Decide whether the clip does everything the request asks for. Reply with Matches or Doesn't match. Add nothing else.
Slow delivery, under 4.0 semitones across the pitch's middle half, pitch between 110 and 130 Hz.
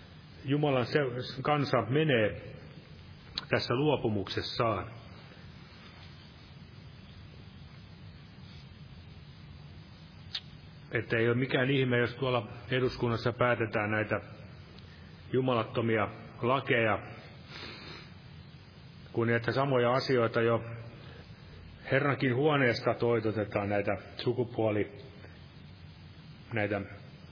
Matches